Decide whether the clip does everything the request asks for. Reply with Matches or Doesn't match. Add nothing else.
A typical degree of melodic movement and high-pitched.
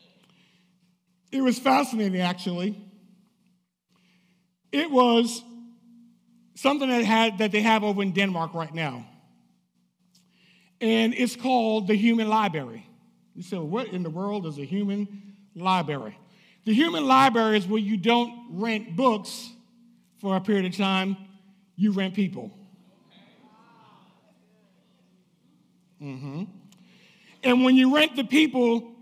Matches